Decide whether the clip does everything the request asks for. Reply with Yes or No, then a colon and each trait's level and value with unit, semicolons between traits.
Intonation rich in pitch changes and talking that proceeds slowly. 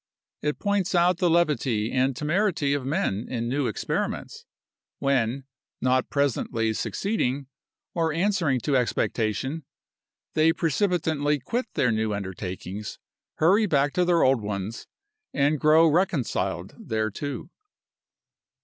Yes: wide, 5.9 semitones; slow, 115 wpm